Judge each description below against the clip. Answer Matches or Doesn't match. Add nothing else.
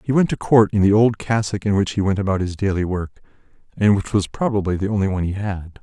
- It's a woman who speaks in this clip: Doesn't match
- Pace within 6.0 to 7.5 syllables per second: Matches